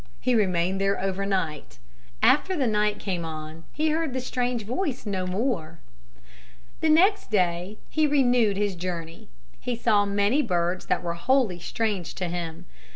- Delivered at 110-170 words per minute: Yes, average, 155 wpm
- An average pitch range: No, wide, 6.0 semitones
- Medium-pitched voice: No, high, 200 Hz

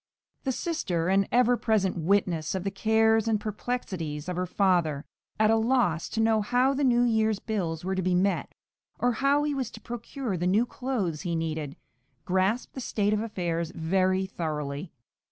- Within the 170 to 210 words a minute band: Yes, average, 180 wpm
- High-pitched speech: Yes, high, 200 Hz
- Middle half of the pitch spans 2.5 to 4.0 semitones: No, average, 4.8 semitones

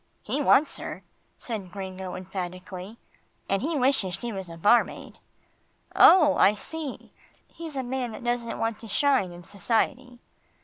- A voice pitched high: Yes, high, 225 Hz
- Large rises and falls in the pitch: Yes, wide, 5.8 semitones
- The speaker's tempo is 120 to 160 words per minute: Yes, average, 145 wpm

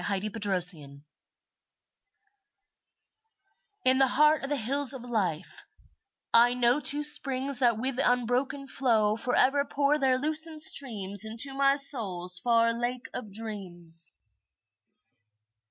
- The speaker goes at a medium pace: No, slow, 115 wpm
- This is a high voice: Yes, high, 245 Hz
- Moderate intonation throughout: Yes, average, 4.7 semitones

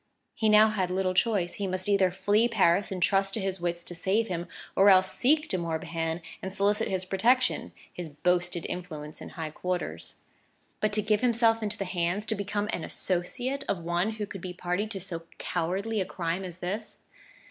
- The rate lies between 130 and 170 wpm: No, average, 195 wpm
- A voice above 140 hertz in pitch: Yes, high, 190 Hz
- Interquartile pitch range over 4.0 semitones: No, average, 3.2 semitones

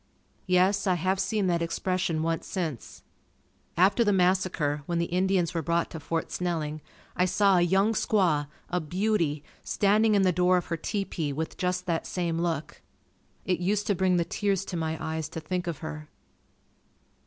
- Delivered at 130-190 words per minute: Yes, average, 175 wpm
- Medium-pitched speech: Yes, medium, 180 Hz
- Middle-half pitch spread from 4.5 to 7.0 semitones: No, average, 2.7 semitones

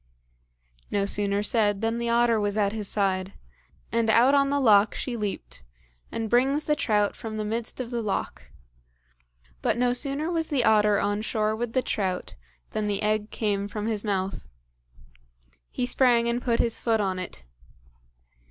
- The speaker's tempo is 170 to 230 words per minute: Yes, average, 175 wpm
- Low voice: No, high, 220 Hz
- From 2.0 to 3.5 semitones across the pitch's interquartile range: Yes, average, 2.7 semitones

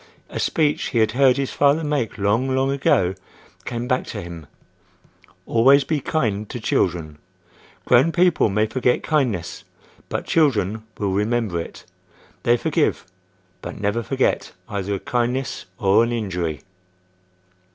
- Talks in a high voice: No, low, 115 Hz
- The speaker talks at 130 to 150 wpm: Yes, average, 140 wpm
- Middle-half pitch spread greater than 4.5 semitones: Yes, average, 4.9 semitones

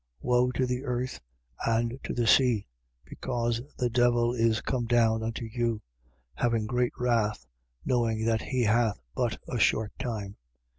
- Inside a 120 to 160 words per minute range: Yes, average, 150 wpm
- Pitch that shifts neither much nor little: No, narrow, 1.7 semitones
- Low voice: Yes, low, 120 Hz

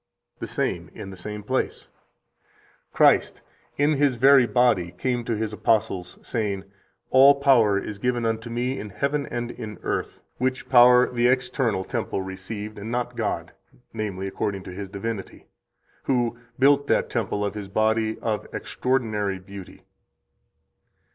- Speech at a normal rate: Yes, average, 150 wpm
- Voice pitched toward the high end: No, low, 115 Hz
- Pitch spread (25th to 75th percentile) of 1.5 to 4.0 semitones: Yes, average, 3.7 semitones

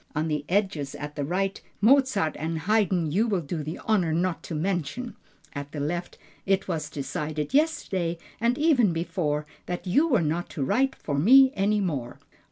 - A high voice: No, medium, 175 Hz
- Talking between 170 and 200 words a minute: Yes, average, 175 wpm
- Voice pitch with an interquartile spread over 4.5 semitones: Yes, wide, 5.5 semitones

